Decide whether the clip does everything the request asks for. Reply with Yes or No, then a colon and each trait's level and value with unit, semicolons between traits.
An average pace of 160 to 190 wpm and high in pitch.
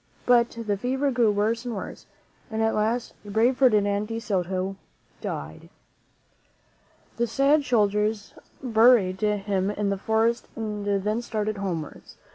No: slow, 135 wpm; high, 215 Hz